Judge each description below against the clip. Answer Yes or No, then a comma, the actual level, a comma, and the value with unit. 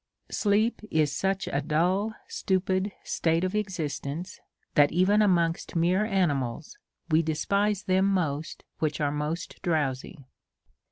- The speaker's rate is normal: No, slow, 120 wpm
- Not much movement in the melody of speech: No, average, 4.2 semitones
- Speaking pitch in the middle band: Yes, medium, 175 Hz